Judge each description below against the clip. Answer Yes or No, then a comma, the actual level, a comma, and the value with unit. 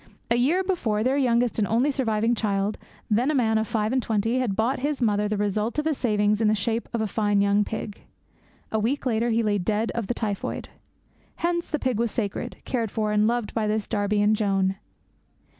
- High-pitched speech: Yes, high, 220 Hz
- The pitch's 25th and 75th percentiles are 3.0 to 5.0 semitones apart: No, narrow, 2.6 semitones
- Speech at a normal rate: No, fast, 215 wpm